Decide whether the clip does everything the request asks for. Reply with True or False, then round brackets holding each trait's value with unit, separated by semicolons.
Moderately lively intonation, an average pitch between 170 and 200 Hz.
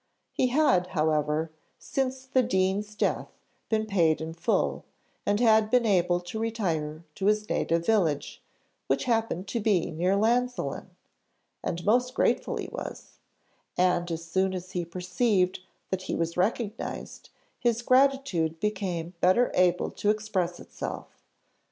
True (4.6 semitones; 190 Hz)